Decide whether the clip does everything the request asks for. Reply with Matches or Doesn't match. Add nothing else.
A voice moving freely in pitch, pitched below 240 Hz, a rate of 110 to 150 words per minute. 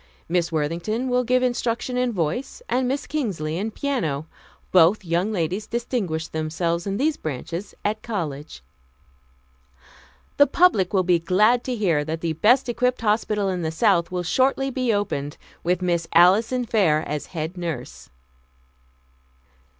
Matches